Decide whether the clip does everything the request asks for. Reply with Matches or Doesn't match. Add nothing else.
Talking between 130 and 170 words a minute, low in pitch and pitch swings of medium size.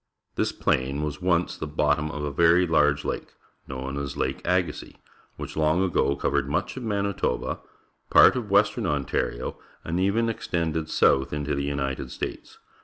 Matches